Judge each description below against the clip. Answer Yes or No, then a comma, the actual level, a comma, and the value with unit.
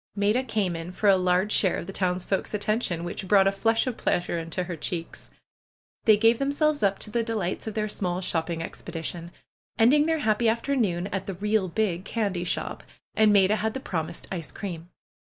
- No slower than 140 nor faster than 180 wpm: No, average, 195 wpm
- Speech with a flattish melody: No, average, 3.8 semitones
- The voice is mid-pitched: No, high, 195 Hz